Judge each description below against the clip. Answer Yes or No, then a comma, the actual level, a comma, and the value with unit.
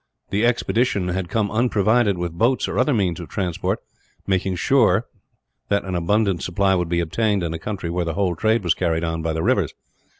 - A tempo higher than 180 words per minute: Yes, average, 200 wpm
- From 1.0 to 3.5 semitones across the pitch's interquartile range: No, average, 4.1 semitones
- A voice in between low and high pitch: No, very low, 95 Hz